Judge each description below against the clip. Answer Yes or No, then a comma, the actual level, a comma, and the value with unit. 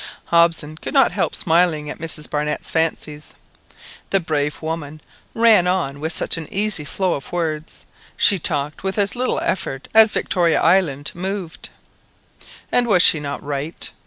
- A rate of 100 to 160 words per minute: Yes, average, 155 wpm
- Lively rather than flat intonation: No, average, 4.0 semitones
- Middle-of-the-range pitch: Yes, medium, 165 Hz